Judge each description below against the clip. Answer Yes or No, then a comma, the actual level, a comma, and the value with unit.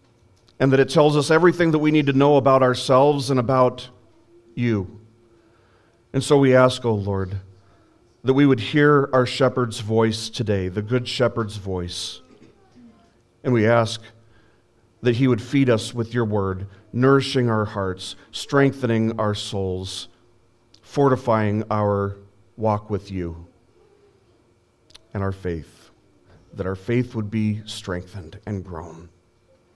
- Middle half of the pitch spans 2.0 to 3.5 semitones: No, average, 4.0 semitones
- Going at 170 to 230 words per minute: No, slow, 135 wpm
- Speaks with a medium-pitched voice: No, low, 115 Hz